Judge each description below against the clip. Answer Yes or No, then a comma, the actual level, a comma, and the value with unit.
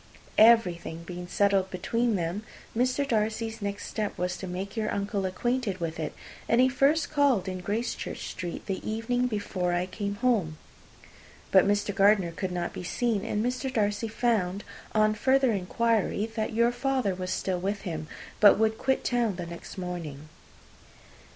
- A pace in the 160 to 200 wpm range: Yes, average, 165 wpm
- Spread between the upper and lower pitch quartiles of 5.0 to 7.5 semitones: No, average, 4.2 semitones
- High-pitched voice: Yes, high, 205 Hz